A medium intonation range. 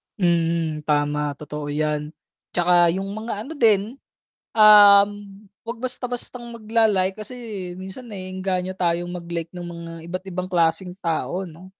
Yes: average, 3.8 semitones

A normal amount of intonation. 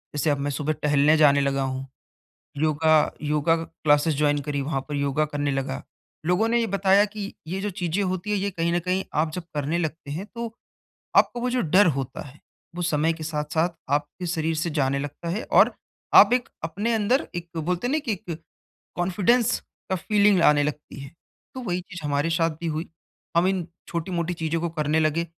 Yes: average, 4.1 semitones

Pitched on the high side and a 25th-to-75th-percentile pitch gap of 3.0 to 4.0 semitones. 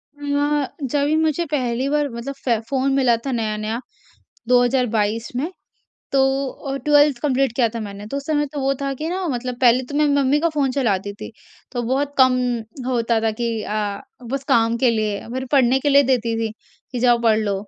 Yes: very high, 255 Hz; average, 3.4 semitones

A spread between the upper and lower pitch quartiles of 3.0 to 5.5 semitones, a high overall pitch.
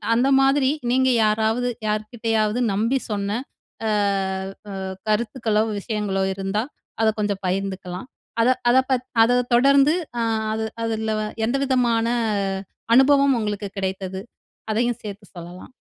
Yes: average, 3.4 semitones; high, 220 Hz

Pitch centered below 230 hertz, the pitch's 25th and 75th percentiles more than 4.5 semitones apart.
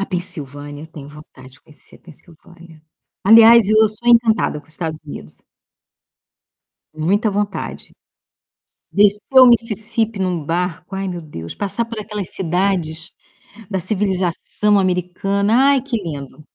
Yes: medium, 185 Hz; average, 4.9 semitones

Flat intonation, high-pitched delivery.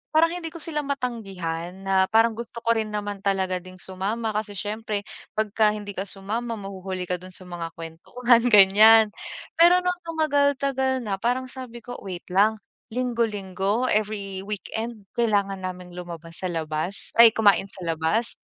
No: average, 3.9 semitones; high, 210 Hz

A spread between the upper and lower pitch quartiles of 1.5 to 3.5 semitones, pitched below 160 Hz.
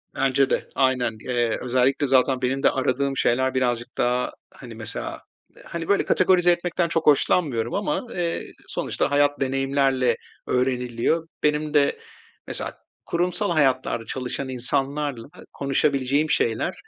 Yes: average, 3.1 semitones; low, 135 Hz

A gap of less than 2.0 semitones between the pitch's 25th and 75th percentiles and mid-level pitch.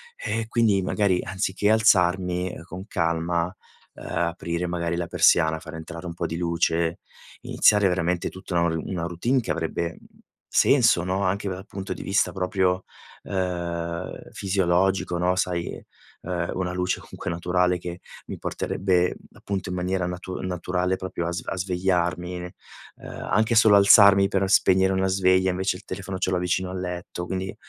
No: narrow, 1.6 semitones; very low, 90 Hz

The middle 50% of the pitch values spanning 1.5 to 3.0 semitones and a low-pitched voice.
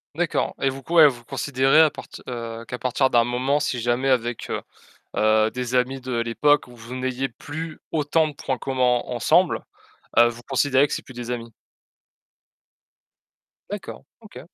Yes: narrow, 2.4 semitones; low, 125 Hz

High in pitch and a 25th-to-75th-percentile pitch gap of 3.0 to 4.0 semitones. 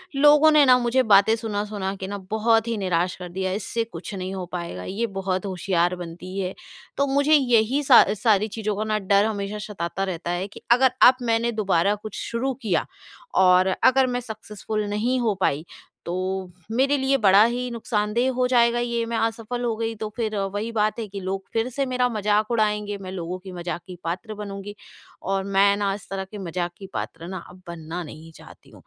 Yes: high, 210 Hz; average, 3.7 semitones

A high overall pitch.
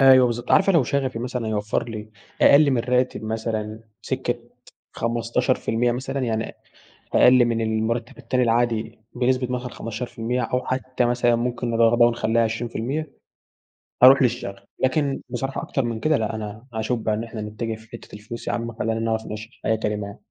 No: low, 115 Hz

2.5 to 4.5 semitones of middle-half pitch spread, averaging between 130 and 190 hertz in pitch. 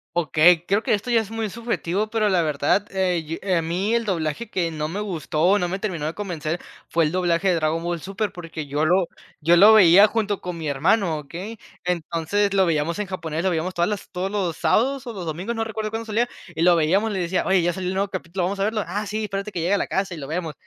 Yes: average, 3.7 semitones; medium, 185 Hz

